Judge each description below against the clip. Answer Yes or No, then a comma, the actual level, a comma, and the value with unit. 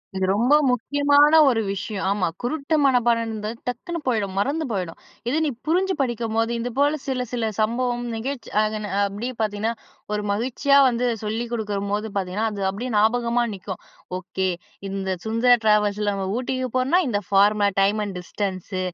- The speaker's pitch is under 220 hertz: No, high, 225 Hz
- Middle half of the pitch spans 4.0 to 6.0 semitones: No, average, 3.6 semitones